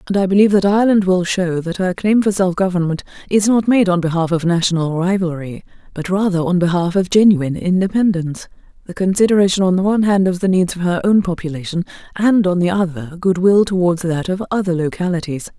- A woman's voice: Yes, female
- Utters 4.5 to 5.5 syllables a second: No, 6.1 syllables/s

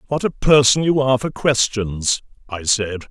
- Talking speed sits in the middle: Yes, average, 175 wpm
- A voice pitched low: Yes, low, 125 Hz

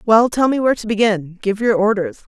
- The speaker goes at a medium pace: No, fast, 230 wpm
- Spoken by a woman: Yes, female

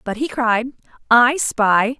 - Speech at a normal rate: Yes, average, 150 wpm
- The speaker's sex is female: Yes, female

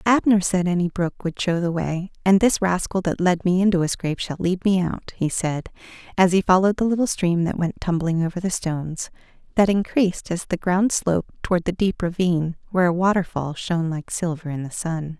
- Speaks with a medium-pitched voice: Yes, medium, 180 Hz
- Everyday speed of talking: No, fast, 215 wpm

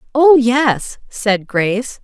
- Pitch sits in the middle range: No, high, 240 Hz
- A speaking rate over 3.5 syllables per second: No, 3.1 syllables/s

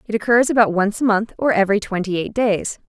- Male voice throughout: No, female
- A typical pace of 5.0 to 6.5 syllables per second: Yes, 6.0 syllables/s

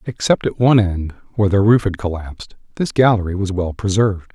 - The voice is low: Yes, low, 100 Hz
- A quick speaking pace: No, average, 195 wpm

